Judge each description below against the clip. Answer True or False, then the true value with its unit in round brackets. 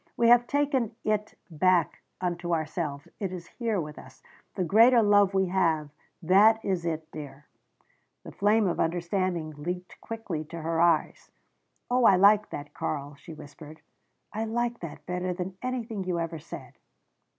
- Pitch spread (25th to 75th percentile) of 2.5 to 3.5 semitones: False (4.7 semitones)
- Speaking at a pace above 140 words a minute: True (160 wpm)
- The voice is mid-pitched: True (180 Hz)